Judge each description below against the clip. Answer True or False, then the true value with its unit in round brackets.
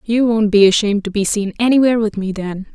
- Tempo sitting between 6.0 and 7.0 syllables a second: True (6.3 syllables/s)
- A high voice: True (210 Hz)